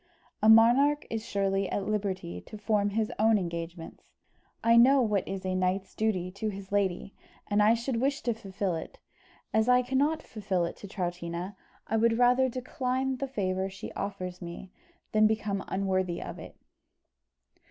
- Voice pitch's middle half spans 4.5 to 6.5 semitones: No, average, 3.7 semitones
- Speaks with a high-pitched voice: Yes, high, 205 Hz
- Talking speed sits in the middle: Yes, average, 165 wpm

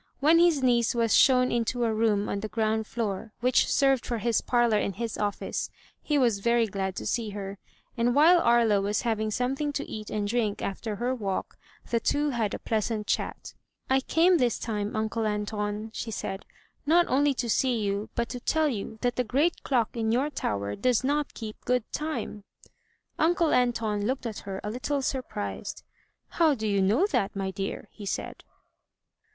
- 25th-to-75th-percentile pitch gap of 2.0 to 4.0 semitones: Yes, average, 3.7 semitones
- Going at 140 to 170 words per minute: No, average, 190 wpm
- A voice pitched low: No, high, 230 Hz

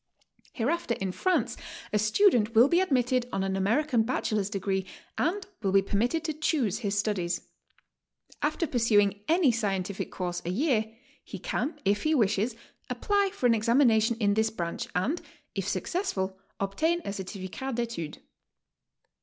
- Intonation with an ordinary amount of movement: No, wide, 6.3 semitones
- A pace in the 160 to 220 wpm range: No, average, 150 wpm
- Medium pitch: No, high, 220 Hz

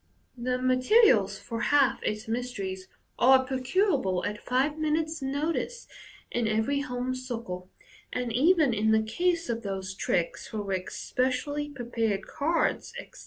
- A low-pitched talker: No, very high, 250 Hz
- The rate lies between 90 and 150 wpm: Yes, average, 140 wpm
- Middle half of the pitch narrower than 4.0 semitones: No, average, 4.9 semitones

